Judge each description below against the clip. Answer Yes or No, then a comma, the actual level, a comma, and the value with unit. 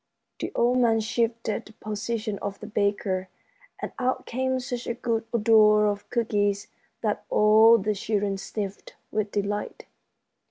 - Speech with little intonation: Yes, narrow, 2.2 semitones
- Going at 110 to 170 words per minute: Yes, average, 145 wpm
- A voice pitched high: Yes, high, 215 Hz